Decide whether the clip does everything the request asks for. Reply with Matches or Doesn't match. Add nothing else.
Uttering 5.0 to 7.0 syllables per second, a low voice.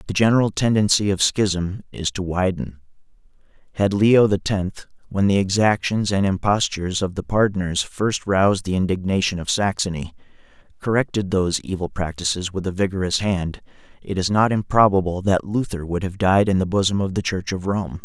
Matches